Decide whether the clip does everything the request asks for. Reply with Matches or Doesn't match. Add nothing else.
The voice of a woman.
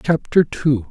Doesn't match